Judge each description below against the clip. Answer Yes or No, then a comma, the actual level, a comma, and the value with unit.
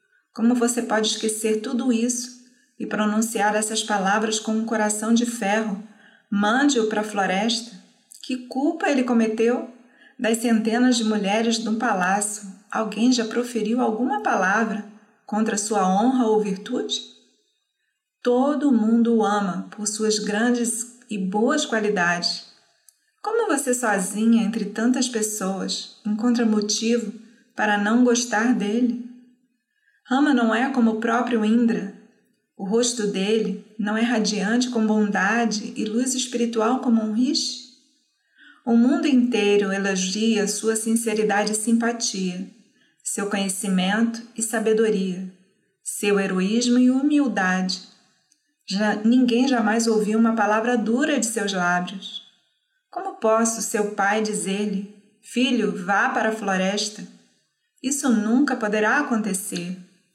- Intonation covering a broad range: No, average, 2.7 semitones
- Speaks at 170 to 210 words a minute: No, slow, 120 wpm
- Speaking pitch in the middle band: No, high, 220 Hz